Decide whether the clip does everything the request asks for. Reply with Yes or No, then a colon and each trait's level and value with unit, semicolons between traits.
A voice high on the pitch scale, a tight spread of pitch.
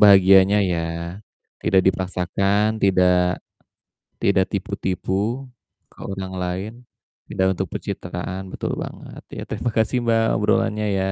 No: very low, 95 Hz; narrow, 2.0 semitones